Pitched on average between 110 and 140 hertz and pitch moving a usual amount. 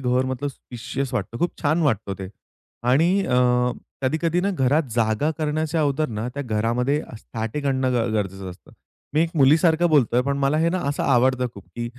Yes: low, 135 Hz; average, 4.5 semitones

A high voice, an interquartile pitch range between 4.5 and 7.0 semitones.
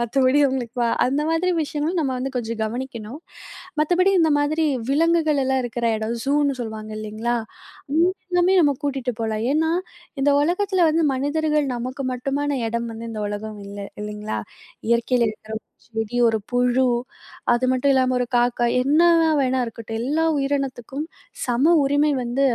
No: very high, 260 Hz; average, 4.1 semitones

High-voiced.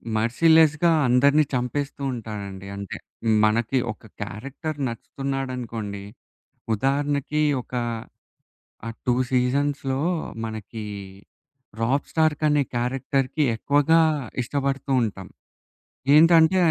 No: low, 135 Hz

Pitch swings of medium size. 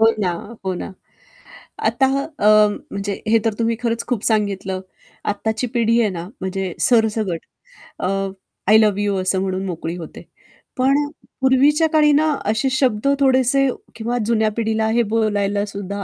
Yes: average, 3.3 semitones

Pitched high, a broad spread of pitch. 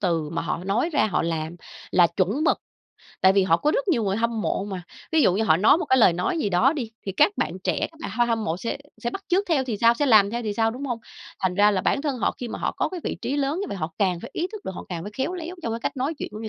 Yes: high, 225 Hz; wide, 6.8 semitones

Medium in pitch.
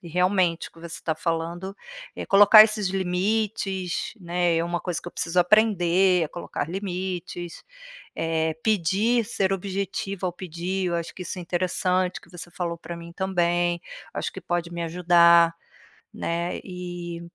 Yes: medium, 175 Hz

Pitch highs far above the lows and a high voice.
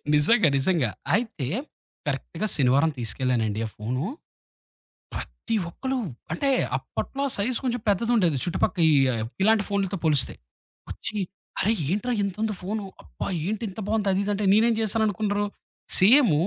Yes: wide, 6.0 semitones; high, 200 Hz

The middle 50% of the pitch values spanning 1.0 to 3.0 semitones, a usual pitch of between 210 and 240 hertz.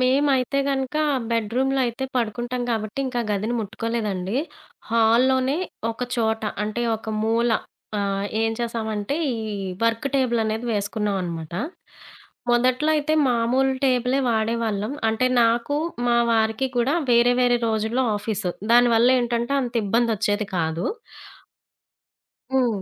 Yes: narrow, 2.5 semitones; high, 235 Hz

